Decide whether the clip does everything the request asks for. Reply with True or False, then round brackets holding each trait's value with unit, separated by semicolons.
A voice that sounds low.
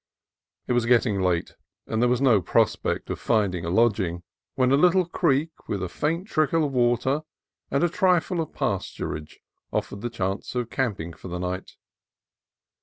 True (120 Hz)